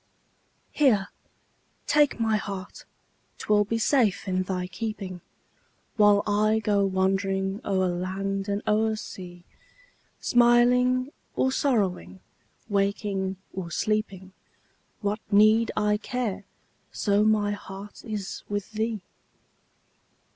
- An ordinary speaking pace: No, slow, 105 wpm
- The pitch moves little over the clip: Yes, narrow, 2.3 semitones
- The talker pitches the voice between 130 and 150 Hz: No, high, 205 Hz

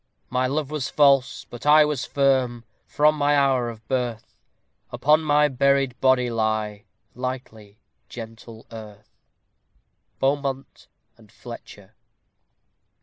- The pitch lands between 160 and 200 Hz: No, low, 130 Hz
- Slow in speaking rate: Yes, slow, 110 wpm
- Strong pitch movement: No, average, 3.6 semitones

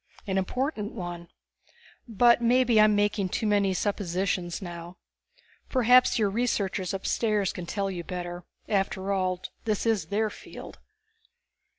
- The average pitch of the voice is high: Yes, high, 200 Hz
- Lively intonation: No, average, 3.2 semitones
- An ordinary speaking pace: No, slow, 125 wpm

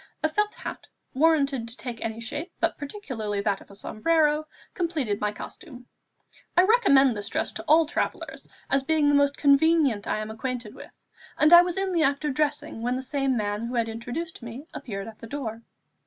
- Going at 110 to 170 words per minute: No, average, 200 wpm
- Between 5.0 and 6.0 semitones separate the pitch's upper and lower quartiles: Yes, wide, 5.5 semitones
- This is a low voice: No, very high, 275 Hz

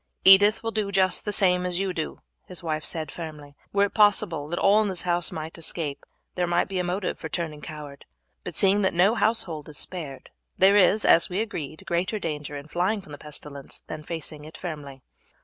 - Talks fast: Yes, fast, 210 wpm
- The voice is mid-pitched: Yes, medium, 175 Hz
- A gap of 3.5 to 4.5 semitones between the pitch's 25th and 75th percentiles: Yes, average, 4.1 semitones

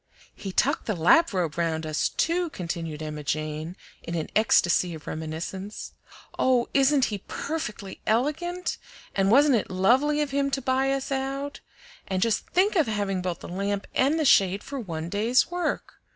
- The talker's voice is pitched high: Yes, high, 210 Hz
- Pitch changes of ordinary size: No, wide, 8.0 semitones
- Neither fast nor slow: Yes, average, 170 wpm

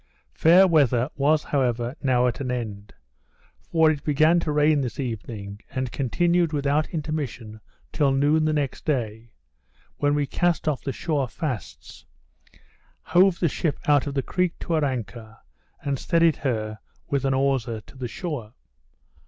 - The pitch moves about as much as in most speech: Yes, average, 4.3 semitones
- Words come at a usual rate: Yes, average, 155 wpm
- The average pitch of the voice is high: No, medium, 140 Hz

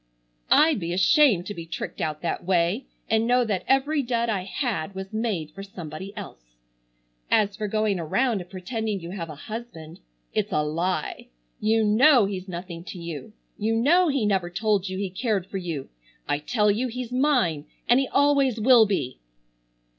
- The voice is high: Yes, high, 200 Hz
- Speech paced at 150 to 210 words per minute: Yes, average, 175 wpm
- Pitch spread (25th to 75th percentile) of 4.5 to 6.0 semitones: Yes, wide, 5.4 semitones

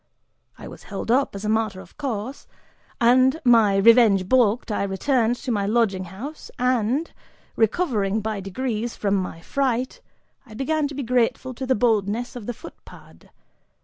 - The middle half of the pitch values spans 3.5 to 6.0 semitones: Yes, average, 4.0 semitones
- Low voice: No, high, 230 Hz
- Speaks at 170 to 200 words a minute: No, average, 160 wpm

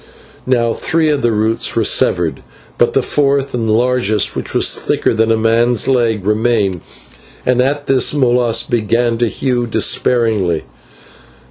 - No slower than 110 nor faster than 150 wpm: Yes, average, 145 wpm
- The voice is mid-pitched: No, low, 120 Hz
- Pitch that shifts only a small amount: Yes, narrow, 2.3 semitones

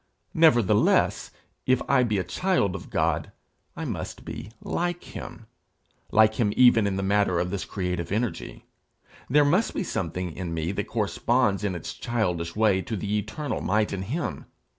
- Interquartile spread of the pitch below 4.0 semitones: No, average, 4.7 semitones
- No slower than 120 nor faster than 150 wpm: No, average, 165 wpm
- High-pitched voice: No, low, 105 Hz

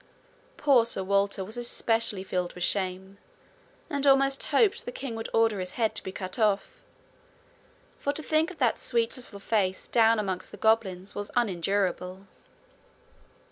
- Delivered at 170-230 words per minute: No, average, 155 wpm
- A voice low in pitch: No, high, 215 Hz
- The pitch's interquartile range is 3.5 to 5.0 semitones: Yes, average, 4.2 semitones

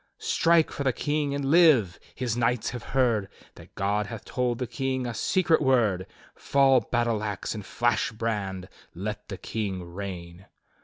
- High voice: No, low, 115 Hz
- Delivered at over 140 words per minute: Yes, average, 160 wpm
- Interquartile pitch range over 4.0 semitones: Yes, average, 4.7 semitones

